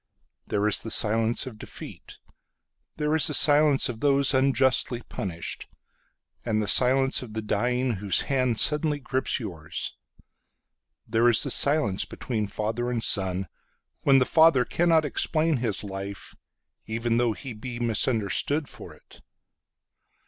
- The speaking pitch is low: Yes, low, 120 Hz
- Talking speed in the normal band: No, slow, 120 wpm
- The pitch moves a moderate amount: Yes, average, 4.3 semitones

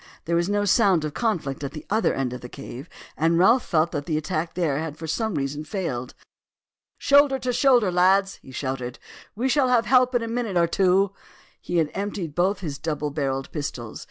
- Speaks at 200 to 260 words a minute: Yes, fast, 205 wpm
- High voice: No, medium, 170 Hz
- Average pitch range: No, wide, 6.0 semitones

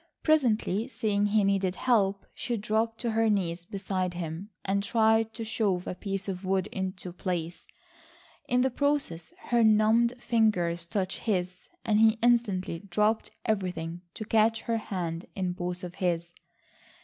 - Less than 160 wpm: Yes, average, 150 wpm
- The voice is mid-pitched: No, high, 200 Hz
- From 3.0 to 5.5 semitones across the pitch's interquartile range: Yes, average, 3.6 semitones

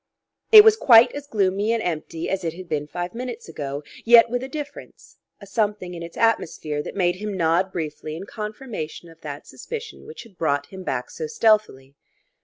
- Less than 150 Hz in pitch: No, high, 190 Hz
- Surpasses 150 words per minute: Yes, average, 195 wpm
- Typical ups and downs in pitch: No, wide, 6.1 semitones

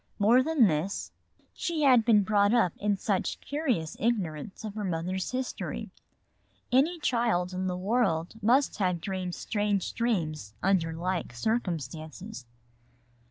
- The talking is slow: Yes, slow, 130 wpm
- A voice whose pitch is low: No, high, 200 Hz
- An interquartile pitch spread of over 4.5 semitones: Yes, average, 5.3 semitones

